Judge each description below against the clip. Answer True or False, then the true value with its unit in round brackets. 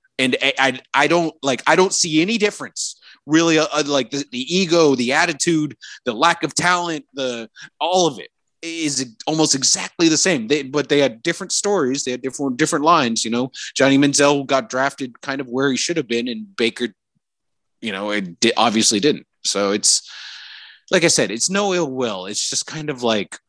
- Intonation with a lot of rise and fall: False (4.6 semitones)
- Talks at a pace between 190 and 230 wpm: True (195 wpm)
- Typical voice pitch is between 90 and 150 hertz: True (140 Hz)